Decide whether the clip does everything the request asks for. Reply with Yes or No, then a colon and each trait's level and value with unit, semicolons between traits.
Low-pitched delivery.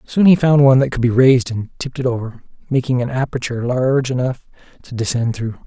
Yes: low, 125 Hz